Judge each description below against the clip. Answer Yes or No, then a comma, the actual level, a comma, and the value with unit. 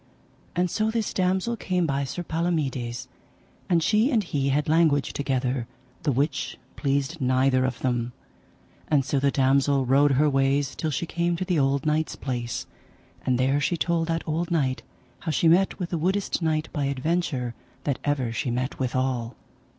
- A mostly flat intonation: No, average, 4.2 semitones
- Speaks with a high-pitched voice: No, medium, 145 Hz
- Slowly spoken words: No, average, 175 wpm